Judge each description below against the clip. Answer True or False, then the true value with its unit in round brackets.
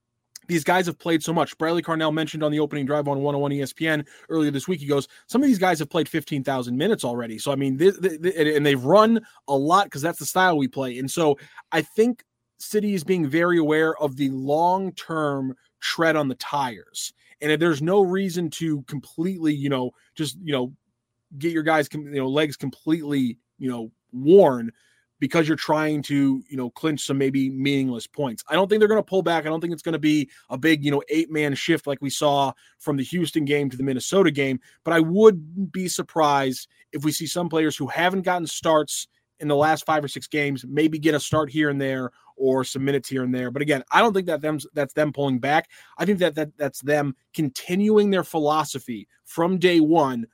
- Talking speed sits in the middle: False (220 wpm)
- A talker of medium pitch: True (150 Hz)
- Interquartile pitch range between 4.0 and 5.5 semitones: False (3.2 semitones)